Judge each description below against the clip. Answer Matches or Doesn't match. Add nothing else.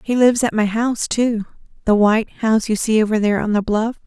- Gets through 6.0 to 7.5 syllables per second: Matches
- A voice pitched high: Matches